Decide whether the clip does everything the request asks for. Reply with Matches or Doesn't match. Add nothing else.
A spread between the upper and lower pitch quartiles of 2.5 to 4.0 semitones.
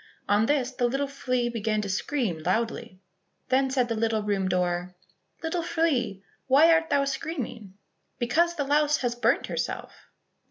Doesn't match